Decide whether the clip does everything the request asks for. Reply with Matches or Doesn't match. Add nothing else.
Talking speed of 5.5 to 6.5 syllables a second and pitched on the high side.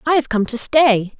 Doesn't match